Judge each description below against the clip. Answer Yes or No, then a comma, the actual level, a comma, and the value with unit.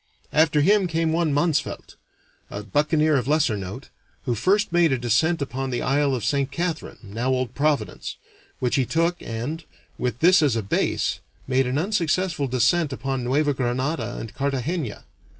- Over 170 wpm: No, average, 165 wpm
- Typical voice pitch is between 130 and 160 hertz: Yes, medium, 140 Hz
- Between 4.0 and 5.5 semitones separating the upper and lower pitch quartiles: Yes, average, 4.4 semitones